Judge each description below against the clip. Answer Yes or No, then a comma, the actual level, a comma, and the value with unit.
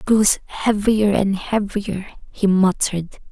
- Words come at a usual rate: No, slow, 125 wpm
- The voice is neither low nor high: No, high, 200 Hz